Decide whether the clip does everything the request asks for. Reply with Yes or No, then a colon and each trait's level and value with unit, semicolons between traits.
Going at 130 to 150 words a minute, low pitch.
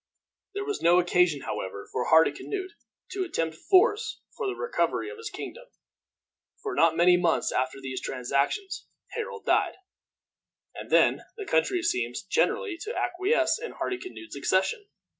No: average, 140 wpm; very high, 365 Hz